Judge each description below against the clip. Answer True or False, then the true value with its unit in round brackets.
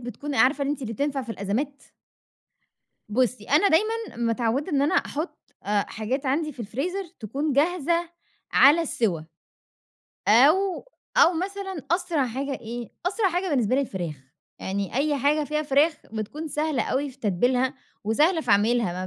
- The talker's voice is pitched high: True (275 Hz)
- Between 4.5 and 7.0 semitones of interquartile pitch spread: True (5.4 semitones)